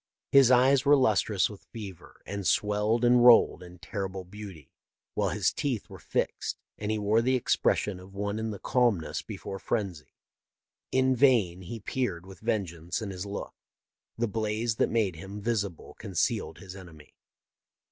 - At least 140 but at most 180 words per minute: Yes, average, 160 wpm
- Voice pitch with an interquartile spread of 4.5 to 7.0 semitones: No, average, 3.8 semitones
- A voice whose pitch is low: Yes, low, 105 Hz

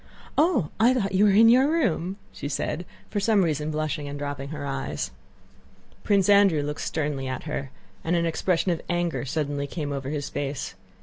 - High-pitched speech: No, medium, 160 Hz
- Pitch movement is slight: No, wide, 5.5 semitones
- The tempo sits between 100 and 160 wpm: No, average, 185 wpm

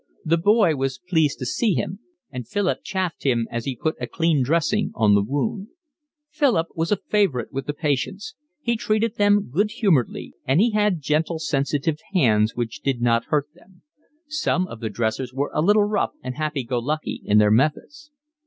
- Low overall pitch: No, medium, 155 Hz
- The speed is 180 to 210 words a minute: Yes, average, 190 wpm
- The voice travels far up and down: Yes, wide, 7.7 semitones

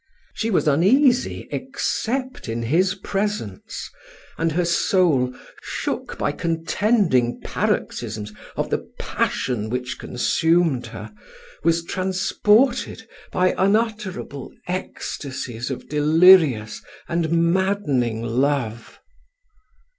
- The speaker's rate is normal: No, slow, 90 wpm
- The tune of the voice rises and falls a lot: Yes, wide, 7.4 semitones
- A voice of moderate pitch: Yes, medium, 165 Hz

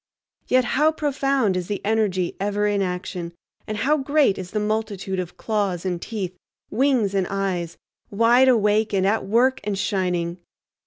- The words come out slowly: No, average, 160 wpm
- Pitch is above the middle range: Yes, high, 205 Hz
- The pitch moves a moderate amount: Yes, average, 3.7 semitones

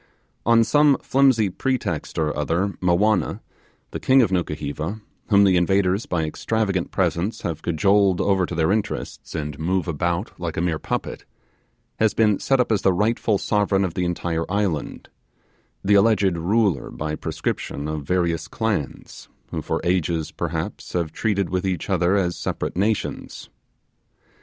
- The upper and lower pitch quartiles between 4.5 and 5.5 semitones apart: No, average, 3.8 semitones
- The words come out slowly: No, average, 150 wpm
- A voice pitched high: No, very low, 95 Hz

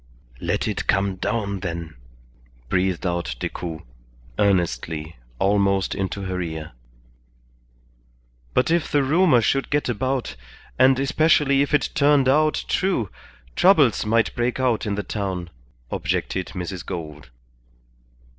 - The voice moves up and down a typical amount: No, wide, 7.3 semitones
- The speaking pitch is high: No, low, 100 Hz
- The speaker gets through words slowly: Yes, slow, 120 wpm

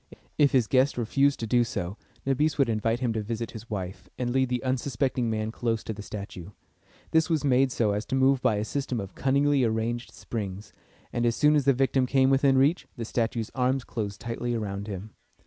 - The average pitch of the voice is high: No, low, 120 Hz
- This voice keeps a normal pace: No, fast, 210 wpm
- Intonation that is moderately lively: Yes, average, 3.5 semitones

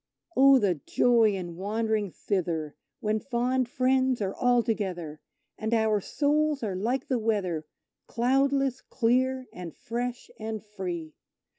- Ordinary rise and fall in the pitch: Yes, average, 4.9 semitones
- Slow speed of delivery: Yes, slow, 130 wpm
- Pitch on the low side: No, high, 225 Hz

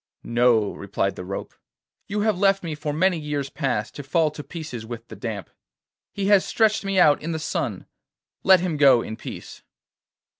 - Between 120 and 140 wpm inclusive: No, average, 185 wpm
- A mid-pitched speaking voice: Yes, medium, 150 Hz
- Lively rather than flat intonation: Yes, wide, 7.6 semitones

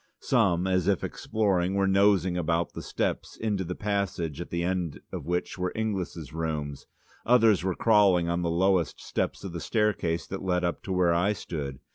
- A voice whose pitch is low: Yes, very low, 90 Hz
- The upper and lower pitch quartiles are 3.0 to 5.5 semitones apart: No, narrow, 2.6 semitones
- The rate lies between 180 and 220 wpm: Yes, average, 185 wpm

